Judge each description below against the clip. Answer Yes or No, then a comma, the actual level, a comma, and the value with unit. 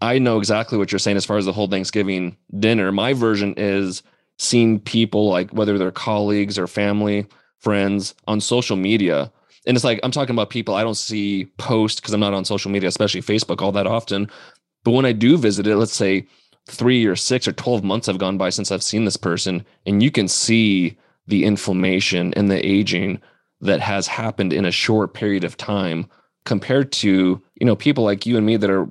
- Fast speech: Yes, fast, 210 wpm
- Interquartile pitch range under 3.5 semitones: Yes, narrow, 2.4 semitones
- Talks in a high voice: No, low, 105 Hz